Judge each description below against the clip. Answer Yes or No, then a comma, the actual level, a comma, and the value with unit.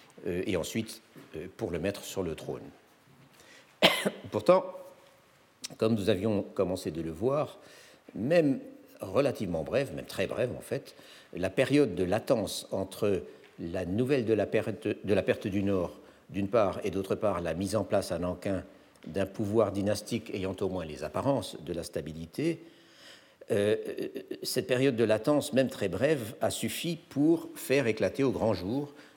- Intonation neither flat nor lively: No, wide, 7.1 semitones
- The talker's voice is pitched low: Yes, low, 110 Hz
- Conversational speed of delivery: Yes, average, 160 wpm